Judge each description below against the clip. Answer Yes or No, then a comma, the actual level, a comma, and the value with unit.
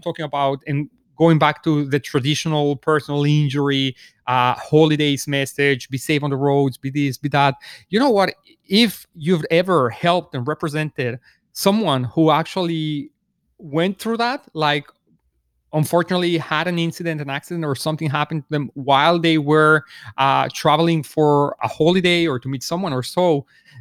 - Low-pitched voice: No, medium, 150 Hz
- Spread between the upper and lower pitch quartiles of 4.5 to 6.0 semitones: No, average, 3.0 semitones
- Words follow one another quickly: No, average, 160 wpm